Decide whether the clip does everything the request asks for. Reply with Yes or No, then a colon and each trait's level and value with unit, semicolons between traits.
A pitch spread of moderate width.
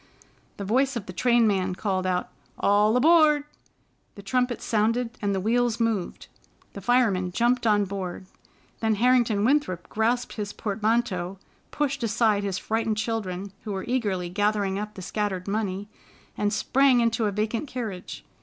Yes: average, 3.4 semitones